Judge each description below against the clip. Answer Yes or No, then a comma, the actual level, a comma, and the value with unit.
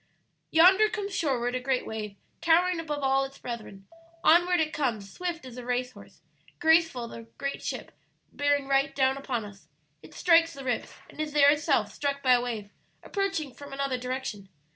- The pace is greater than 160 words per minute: Yes, average, 185 wpm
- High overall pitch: Yes, very high, 275 Hz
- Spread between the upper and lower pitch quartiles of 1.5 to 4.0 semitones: No, average, 4.5 semitones